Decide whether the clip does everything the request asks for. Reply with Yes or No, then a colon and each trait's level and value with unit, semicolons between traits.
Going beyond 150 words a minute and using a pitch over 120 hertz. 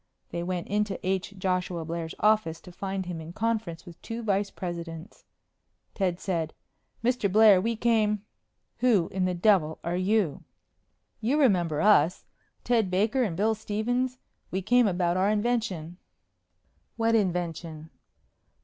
No: average, 140 wpm; high, 190 Hz